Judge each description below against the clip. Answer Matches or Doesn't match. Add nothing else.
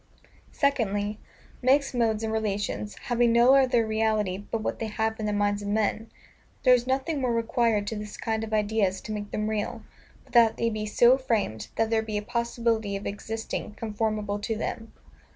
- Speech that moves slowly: Doesn't match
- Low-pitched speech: Doesn't match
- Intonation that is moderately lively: Doesn't match